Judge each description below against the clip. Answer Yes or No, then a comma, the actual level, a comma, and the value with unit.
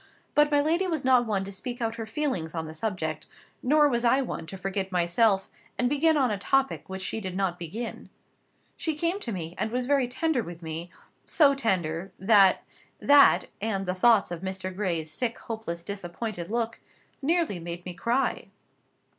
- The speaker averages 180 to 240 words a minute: Yes, average, 185 wpm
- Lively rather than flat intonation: Yes, wide, 6.3 semitones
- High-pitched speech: Yes, high, 215 Hz